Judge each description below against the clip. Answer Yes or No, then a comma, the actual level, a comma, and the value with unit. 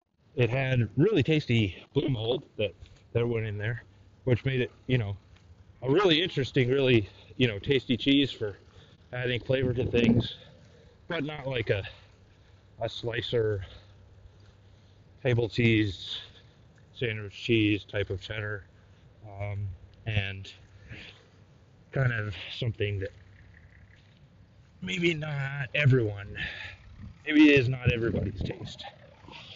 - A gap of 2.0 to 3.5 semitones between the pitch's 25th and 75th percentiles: No, average, 4.2 semitones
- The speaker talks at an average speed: No, slow, 115 wpm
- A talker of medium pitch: No, low, 110 Hz